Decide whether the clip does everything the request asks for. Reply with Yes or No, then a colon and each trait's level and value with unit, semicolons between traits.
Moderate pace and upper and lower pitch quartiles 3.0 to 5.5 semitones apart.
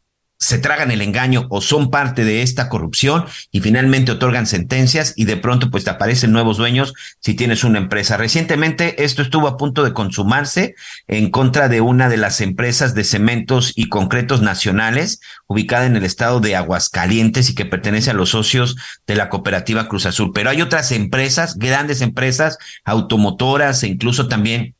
Yes: average, 175 wpm; average, 3.9 semitones